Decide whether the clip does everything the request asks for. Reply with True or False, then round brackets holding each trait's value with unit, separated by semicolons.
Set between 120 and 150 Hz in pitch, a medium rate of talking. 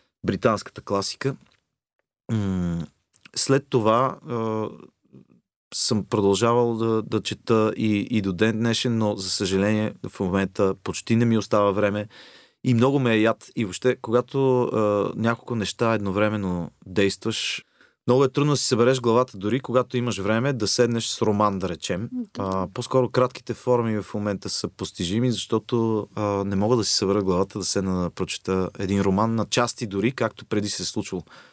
False (110 Hz; 155 wpm)